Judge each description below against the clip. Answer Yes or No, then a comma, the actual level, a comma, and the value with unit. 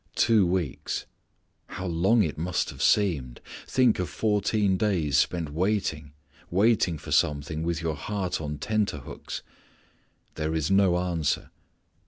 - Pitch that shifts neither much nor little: Yes, average, 4.6 semitones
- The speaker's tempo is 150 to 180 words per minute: No, slow, 135 wpm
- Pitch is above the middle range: No, very low, 90 Hz